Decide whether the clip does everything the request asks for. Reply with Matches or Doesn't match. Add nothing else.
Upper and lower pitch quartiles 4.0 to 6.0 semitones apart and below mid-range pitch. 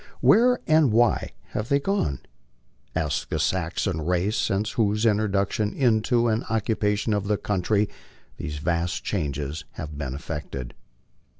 Matches